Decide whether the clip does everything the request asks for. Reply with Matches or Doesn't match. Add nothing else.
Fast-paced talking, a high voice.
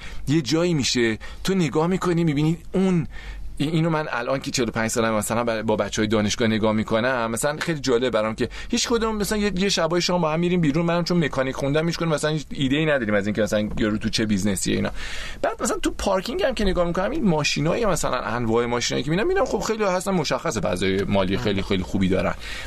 Doesn't match